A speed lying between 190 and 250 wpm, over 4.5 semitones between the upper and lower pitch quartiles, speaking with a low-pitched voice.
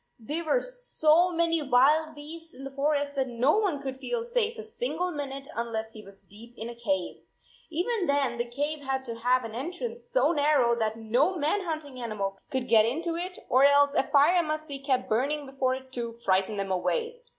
No: fast, 205 wpm; wide, 5.6 semitones; very high, 280 Hz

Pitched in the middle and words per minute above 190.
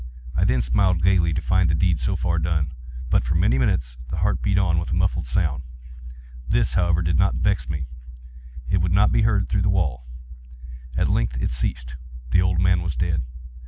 No: very low, 85 Hz; average, 200 wpm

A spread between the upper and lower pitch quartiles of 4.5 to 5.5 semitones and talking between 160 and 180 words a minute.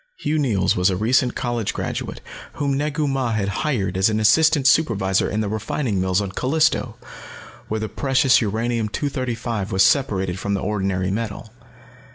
Yes: average, 5.2 semitones; average, 165 wpm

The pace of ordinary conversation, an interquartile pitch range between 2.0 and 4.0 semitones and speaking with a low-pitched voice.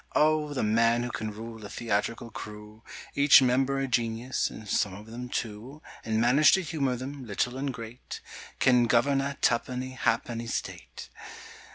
Yes: average, 165 wpm; average, 3.2 semitones; low, 120 Hz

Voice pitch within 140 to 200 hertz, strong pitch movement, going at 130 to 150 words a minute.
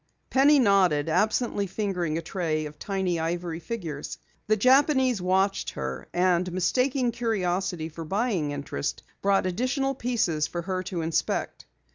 Yes: medium, 185 Hz; wide, 5.7 semitones; slow, 135 wpm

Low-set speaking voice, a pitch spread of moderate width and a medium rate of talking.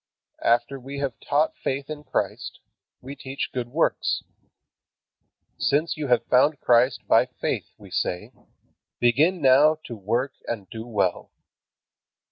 No: low, 130 Hz; average, 3.3 semitones; slow, 130 wpm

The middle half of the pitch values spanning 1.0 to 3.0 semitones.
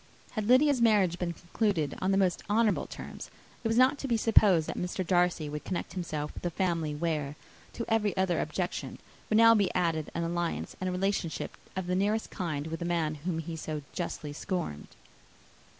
No: average, 4.1 semitones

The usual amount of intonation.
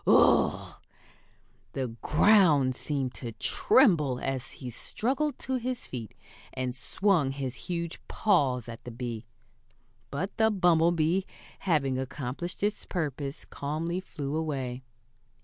No: wide, 5.7 semitones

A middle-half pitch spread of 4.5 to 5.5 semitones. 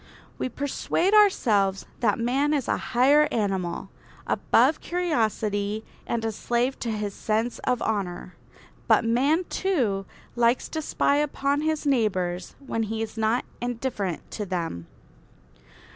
Yes: average, 5.2 semitones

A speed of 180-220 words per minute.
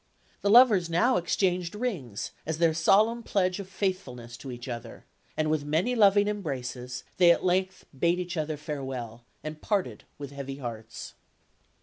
No: average, 155 wpm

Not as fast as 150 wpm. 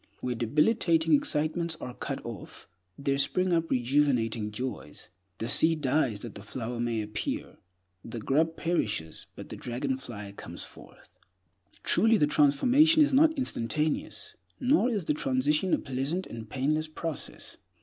Yes: average, 140 wpm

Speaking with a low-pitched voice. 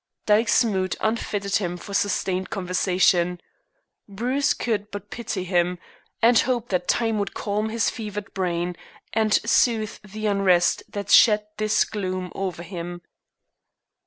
No: high, 200 Hz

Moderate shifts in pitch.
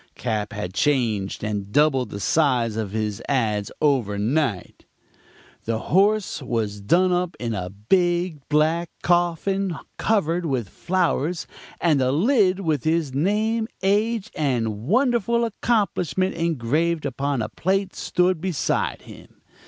No: wide, 8.2 semitones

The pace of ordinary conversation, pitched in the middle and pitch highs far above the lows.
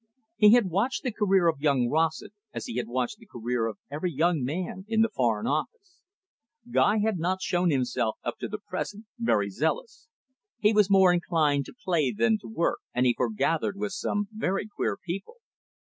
Yes: average, 190 wpm; medium, 180 Hz; wide, 7.1 semitones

